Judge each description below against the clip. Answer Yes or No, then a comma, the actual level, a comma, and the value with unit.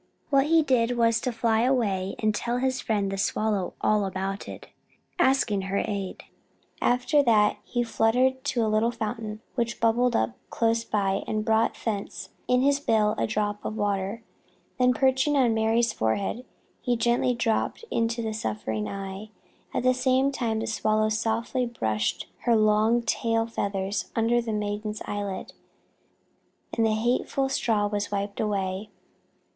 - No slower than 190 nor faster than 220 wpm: No, average, 160 wpm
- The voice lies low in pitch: No, high, 225 Hz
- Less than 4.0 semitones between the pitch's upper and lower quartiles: Yes, average, 2.7 semitones